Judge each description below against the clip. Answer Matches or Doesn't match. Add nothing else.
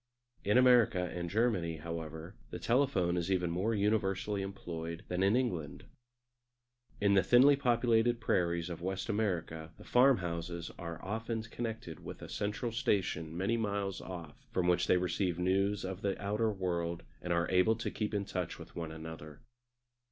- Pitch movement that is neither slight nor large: Matches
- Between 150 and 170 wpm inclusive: Matches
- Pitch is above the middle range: Doesn't match